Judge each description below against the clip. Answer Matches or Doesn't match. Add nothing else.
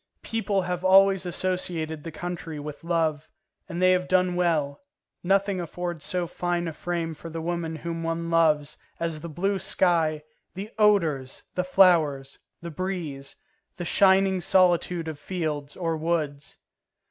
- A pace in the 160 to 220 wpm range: Doesn't match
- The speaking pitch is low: Doesn't match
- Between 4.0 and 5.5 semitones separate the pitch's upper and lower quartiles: Doesn't match